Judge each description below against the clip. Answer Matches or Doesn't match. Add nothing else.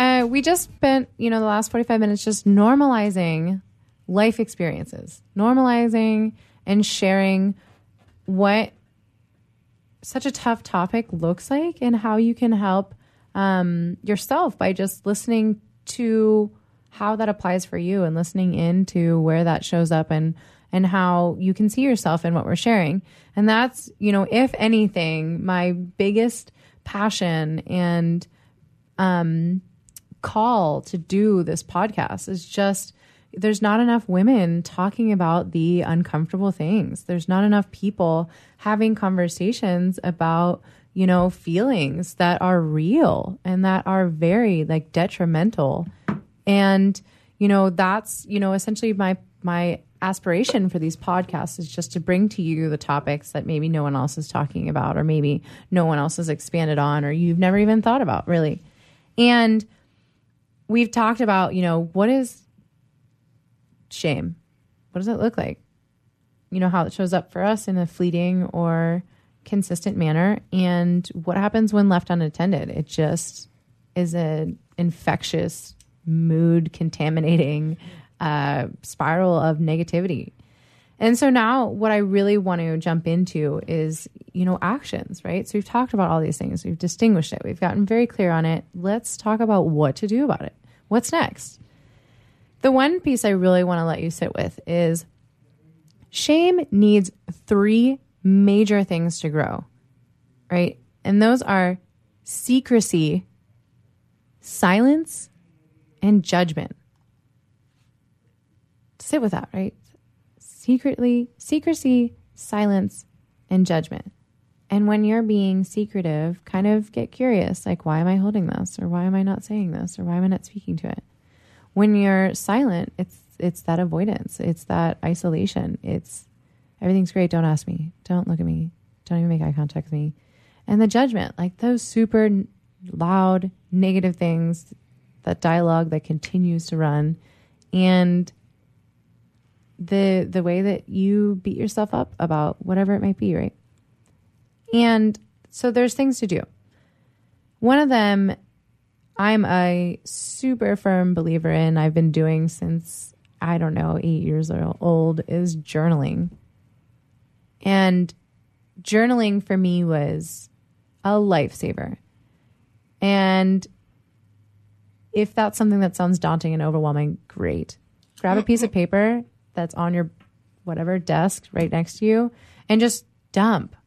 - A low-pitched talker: Doesn't match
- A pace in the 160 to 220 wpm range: Doesn't match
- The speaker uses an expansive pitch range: Doesn't match